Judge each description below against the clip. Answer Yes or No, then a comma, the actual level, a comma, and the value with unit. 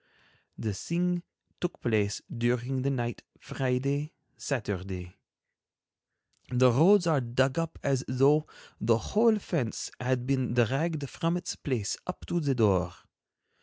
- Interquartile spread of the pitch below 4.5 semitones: No, average, 4.8 semitones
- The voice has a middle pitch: No, low, 130 Hz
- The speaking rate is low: Yes, slow, 125 wpm